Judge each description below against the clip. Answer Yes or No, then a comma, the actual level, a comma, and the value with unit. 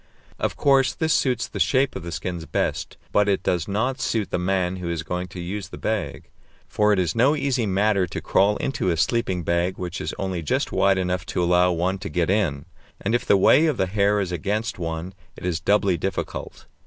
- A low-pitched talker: Yes, very low, 95 Hz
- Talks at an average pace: No, fast, 220 wpm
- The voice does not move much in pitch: No, average, 3.1 semitones